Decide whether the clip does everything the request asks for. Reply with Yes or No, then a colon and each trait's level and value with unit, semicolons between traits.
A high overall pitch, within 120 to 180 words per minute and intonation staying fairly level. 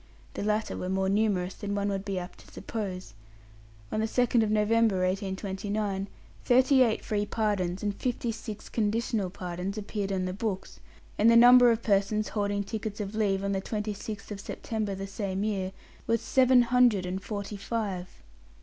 Yes: high, 205 Hz; average, 170 wpm; narrow, 2.3 semitones